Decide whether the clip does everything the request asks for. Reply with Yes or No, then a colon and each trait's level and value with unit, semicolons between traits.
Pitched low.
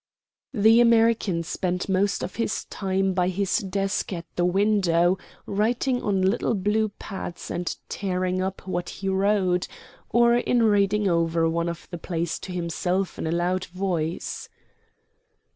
No: high, 190 Hz